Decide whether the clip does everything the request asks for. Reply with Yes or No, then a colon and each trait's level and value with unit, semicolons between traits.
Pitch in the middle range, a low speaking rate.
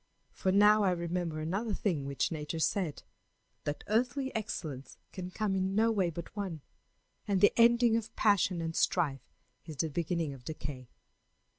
No: medium, 180 Hz; average, 160 wpm